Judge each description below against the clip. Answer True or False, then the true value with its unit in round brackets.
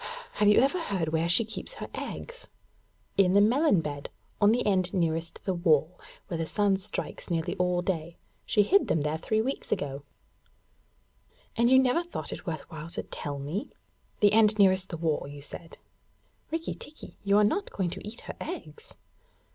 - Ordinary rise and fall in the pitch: True (5.0 semitones)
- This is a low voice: False (190 Hz)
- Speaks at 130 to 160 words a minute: False (180 wpm)